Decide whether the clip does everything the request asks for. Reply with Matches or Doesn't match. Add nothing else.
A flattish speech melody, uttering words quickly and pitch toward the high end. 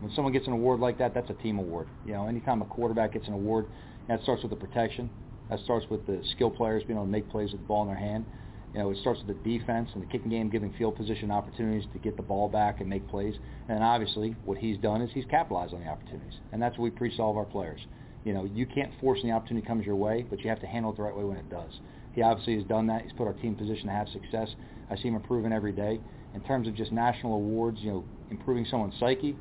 Doesn't match